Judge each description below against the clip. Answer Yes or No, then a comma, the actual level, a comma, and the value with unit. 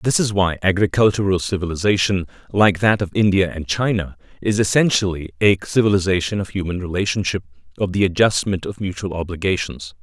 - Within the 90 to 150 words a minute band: Yes, average, 145 wpm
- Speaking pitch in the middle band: No, very low, 95 Hz